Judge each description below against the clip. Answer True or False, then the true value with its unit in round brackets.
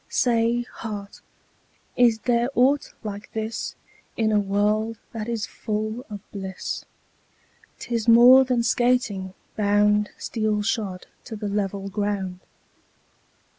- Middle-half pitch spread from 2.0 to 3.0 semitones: True (2.4 semitones)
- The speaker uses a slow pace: True (120 wpm)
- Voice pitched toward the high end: True (215 Hz)